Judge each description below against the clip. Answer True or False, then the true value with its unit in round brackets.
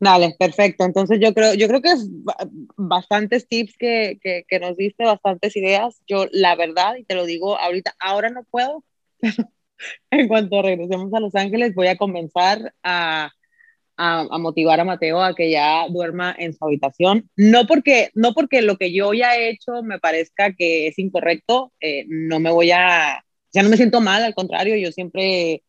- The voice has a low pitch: False (195 Hz)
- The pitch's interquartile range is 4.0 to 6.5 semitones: True (4.3 semitones)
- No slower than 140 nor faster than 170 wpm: False (190 wpm)